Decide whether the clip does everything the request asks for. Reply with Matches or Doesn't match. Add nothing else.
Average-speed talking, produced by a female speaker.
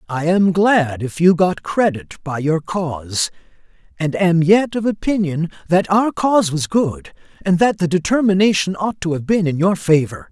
Doesn't match